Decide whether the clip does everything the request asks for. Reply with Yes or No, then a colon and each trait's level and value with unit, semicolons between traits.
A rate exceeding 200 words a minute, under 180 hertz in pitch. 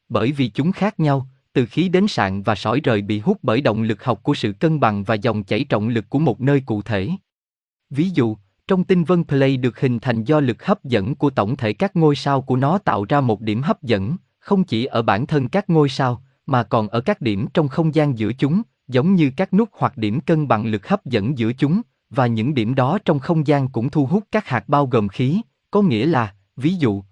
Yes: average, 245 wpm; low, 135 Hz